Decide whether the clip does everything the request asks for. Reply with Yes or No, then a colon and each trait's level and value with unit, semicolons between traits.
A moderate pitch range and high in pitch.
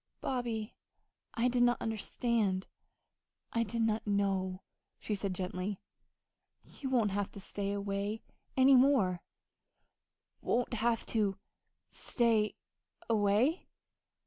Yes: average, 3.2 semitones; high, 215 Hz